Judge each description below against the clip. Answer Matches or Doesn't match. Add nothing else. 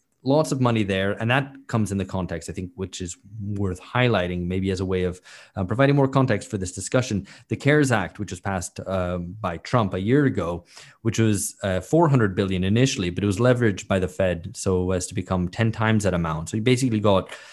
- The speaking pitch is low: Matches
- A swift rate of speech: Matches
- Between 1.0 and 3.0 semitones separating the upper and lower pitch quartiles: Doesn't match